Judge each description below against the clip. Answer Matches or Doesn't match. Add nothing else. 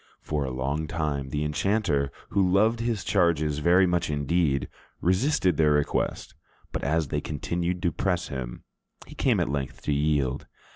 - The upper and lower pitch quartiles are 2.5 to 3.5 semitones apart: Doesn't match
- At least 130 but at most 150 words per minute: Doesn't match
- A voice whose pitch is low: Matches